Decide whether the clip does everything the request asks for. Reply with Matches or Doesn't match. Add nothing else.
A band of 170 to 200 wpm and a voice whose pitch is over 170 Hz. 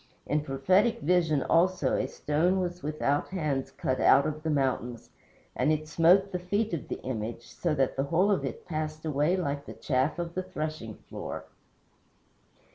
Doesn't match